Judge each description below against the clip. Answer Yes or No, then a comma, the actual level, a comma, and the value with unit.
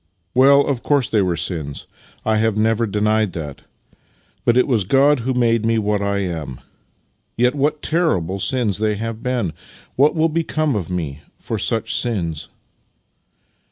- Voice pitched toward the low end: Yes, low, 110 Hz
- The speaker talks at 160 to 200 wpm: Yes, average, 165 wpm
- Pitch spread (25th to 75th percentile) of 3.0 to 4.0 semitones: No, average, 5.3 semitones